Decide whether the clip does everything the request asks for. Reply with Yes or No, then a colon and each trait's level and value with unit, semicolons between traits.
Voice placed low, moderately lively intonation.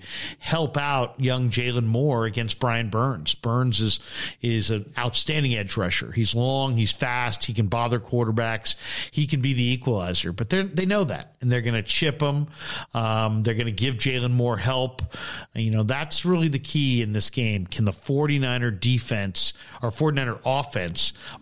Yes: low, 120 Hz; average, 3.4 semitones